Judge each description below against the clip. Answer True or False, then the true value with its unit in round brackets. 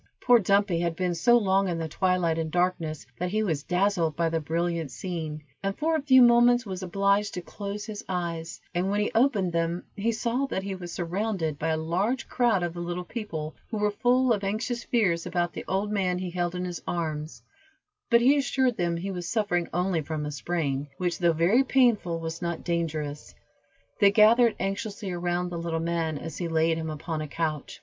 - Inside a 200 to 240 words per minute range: True (205 wpm)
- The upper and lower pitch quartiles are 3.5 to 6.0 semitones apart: True (3.9 semitones)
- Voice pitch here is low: False (180 Hz)